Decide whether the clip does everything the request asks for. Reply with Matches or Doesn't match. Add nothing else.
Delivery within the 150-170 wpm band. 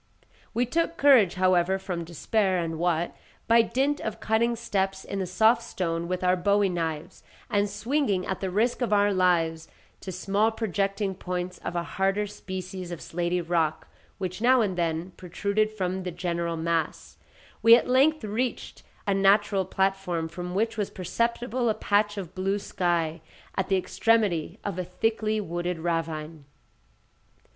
Matches